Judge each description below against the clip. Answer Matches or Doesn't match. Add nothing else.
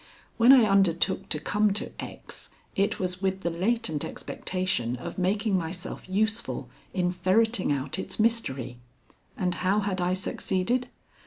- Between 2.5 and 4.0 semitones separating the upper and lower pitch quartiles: Matches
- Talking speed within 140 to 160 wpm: Matches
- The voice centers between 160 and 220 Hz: Matches